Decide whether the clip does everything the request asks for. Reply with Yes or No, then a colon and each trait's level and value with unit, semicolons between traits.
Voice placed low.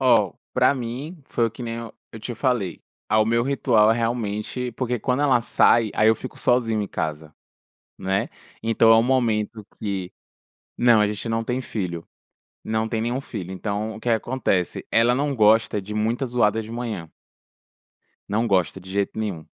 Yes: low, 115 Hz